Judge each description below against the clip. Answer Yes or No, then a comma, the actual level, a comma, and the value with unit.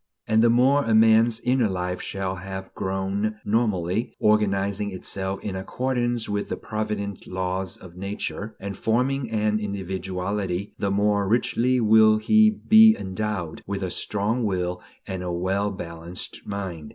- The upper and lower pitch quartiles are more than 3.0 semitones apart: No, average, 2.7 semitones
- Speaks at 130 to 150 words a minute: Yes, average, 145 wpm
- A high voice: No, low, 100 Hz